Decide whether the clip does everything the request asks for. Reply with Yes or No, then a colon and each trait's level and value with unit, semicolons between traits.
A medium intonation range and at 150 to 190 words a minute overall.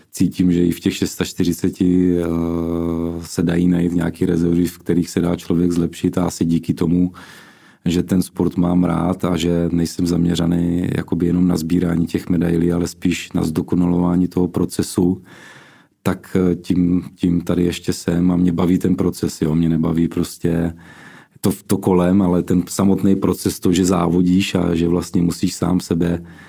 No: narrow, 1.0 semitones; average, 165 wpm